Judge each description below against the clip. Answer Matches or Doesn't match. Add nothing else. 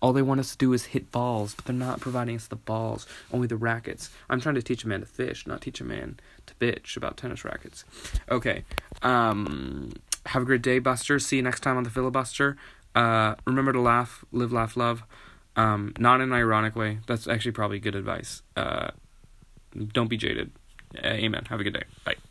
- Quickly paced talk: Matches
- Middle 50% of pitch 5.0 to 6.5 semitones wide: Doesn't match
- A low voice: Matches